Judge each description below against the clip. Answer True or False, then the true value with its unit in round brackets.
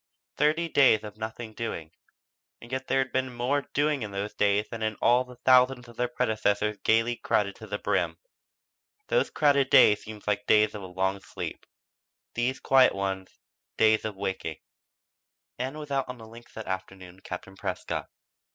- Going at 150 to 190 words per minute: True (180 wpm)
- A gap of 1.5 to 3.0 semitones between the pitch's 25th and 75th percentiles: False (4.1 semitones)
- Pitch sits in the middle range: False (110 Hz)